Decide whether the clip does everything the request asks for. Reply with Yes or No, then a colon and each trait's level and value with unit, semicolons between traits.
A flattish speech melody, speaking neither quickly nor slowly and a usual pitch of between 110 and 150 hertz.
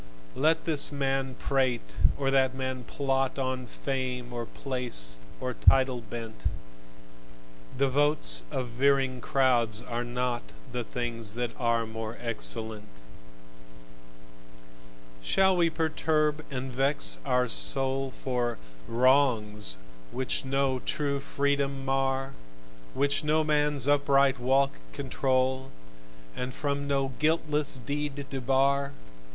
No: narrow, 2.3 semitones; slow, 110 wpm; low, 135 Hz